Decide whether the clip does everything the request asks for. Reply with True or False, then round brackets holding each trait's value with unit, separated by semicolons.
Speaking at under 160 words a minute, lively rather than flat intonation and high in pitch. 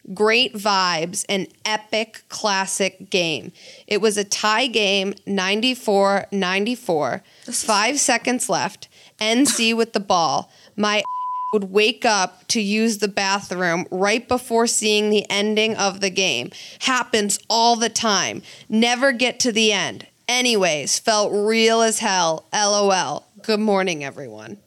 False (135 wpm; 2.8 semitones; 210 Hz)